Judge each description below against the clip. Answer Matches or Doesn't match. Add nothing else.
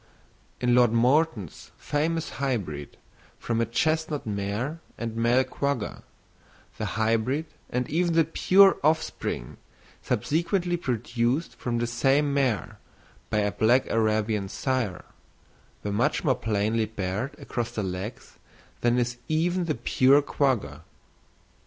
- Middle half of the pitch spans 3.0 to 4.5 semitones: Doesn't match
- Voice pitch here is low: Matches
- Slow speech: Matches